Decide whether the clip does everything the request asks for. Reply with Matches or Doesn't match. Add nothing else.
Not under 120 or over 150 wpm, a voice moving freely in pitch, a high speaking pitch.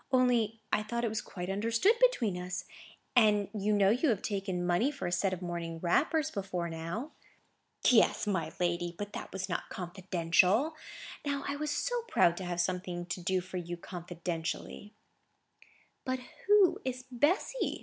Doesn't match